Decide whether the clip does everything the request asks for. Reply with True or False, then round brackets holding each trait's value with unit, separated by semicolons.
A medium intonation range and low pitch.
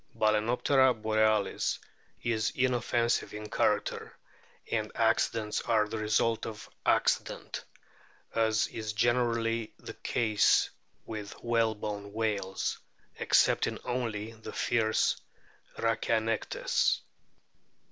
False (1.5 semitones; 110 Hz)